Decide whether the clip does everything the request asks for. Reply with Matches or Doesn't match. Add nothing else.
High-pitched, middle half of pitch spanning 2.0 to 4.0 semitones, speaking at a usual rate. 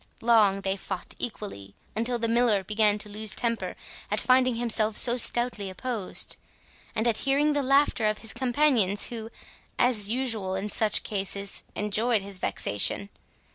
Matches